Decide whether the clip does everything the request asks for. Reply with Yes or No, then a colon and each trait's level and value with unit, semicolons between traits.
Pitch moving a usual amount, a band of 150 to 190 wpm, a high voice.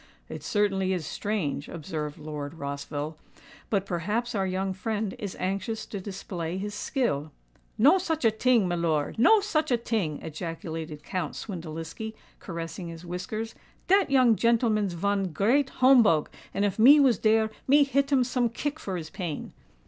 No: wide, 6.0 semitones; average, 155 wpm; high, 200 Hz